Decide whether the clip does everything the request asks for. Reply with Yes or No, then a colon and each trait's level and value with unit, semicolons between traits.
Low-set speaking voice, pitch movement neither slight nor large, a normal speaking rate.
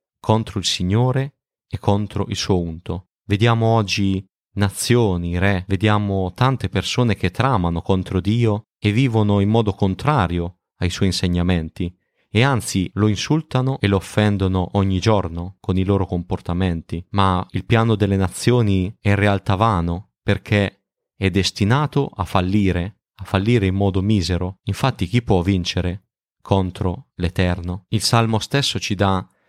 Yes: low, 100 Hz; average, 3.0 semitones; average, 140 wpm